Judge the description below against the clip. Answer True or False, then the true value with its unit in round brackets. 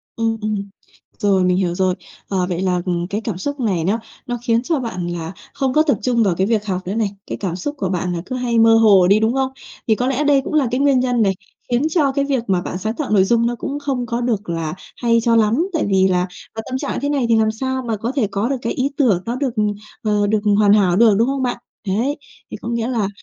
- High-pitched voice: True (225 Hz)